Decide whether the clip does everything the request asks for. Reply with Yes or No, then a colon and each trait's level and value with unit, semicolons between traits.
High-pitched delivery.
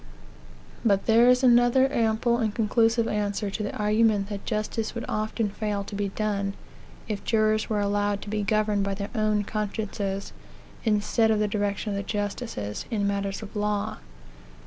Yes: high, 210 Hz